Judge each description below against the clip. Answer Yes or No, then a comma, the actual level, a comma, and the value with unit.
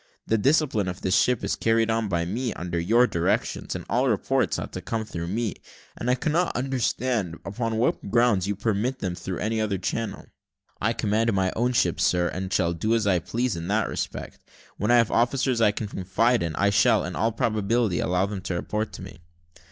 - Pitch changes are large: No, average, 3.9 semitones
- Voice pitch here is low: Yes, low, 110 Hz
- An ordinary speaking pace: No, fast, 210 wpm